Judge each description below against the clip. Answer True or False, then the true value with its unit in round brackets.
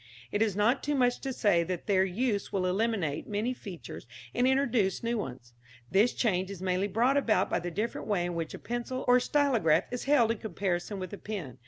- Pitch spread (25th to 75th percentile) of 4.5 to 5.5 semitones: True (4.8 semitones)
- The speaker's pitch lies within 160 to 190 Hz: False (205 Hz)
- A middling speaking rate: False (210 wpm)